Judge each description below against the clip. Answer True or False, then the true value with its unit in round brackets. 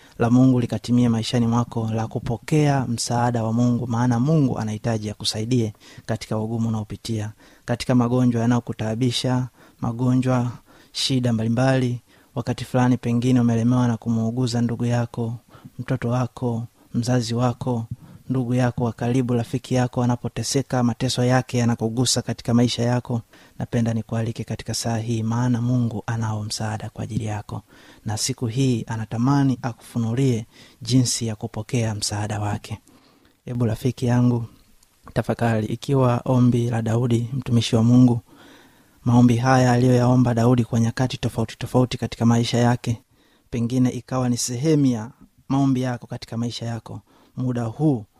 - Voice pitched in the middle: False (120 Hz)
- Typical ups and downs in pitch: False (1.6 semitones)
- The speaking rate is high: False (125 wpm)